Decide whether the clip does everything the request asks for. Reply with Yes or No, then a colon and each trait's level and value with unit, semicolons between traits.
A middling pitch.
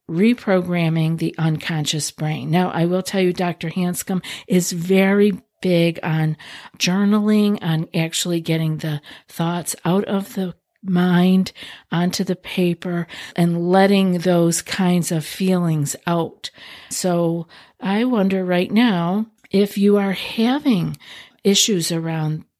Yes: medium, 180 Hz